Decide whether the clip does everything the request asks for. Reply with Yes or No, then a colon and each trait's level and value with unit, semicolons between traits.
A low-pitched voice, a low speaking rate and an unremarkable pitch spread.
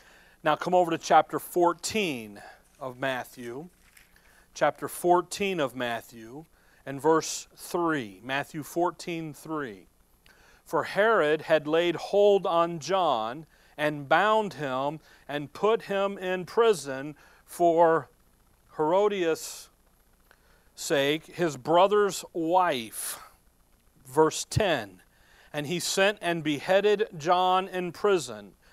No: medium, 160 Hz; slow, 100 wpm; average, 4.7 semitones